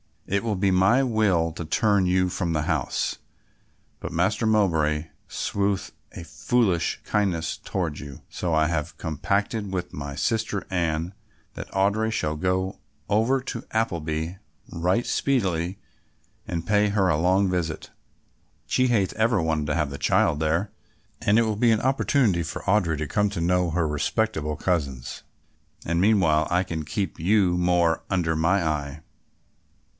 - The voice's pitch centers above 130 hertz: No, very low, 90 Hz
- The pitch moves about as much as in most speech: Yes, average, 4.3 semitones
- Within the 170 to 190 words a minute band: No, average, 155 wpm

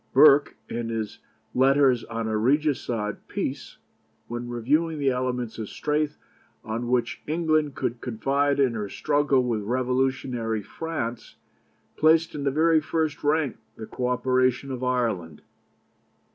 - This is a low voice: Yes, low, 130 Hz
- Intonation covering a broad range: No, average, 3.8 semitones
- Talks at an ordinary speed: No, slow, 130 wpm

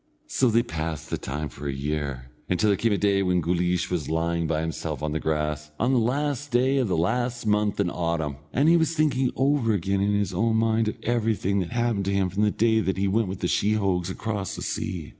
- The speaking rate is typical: No, fast, 235 wpm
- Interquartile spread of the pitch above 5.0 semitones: Yes, wide, 5.4 semitones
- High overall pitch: No, low, 100 Hz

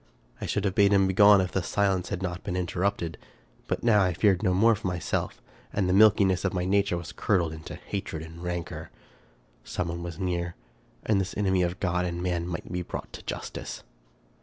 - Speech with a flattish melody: Yes, narrow, 2.2 semitones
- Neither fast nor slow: No, fast, 210 wpm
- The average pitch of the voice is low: Yes, very low, 90 Hz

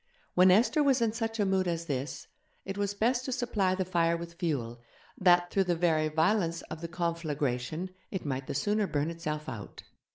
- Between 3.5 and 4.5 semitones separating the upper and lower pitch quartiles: Yes, average, 4.2 semitones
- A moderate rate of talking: Yes, average, 195 wpm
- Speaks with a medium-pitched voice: Yes, medium, 175 Hz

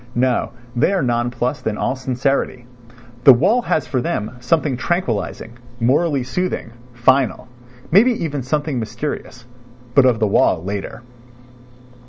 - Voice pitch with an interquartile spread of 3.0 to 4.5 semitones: Yes, average, 3.4 semitones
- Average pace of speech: No, slow, 125 wpm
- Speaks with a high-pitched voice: No, low, 125 Hz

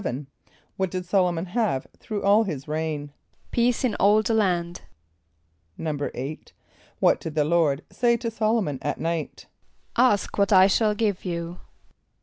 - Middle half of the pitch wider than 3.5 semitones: Yes, average, 5.1 semitones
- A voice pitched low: No, medium, 185 Hz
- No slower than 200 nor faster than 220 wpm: No, average, 155 wpm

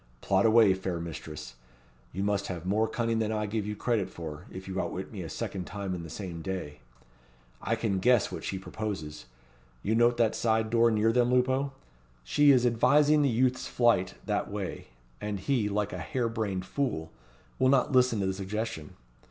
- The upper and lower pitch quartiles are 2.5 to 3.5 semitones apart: No, average, 3.9 semitones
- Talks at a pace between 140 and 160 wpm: No, average, 190 wpm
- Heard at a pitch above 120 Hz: No, low, 105 Hz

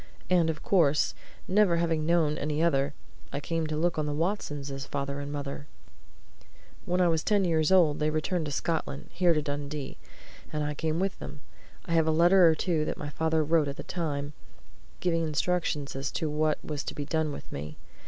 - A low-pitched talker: No, medium, 155 Hz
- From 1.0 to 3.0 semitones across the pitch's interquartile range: Yes, narrow, 2.5 semitones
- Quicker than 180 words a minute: Yes, average, 200 wpm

